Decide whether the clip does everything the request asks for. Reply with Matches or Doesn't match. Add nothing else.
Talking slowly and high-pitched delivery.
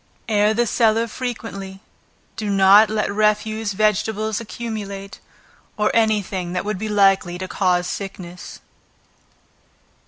Matches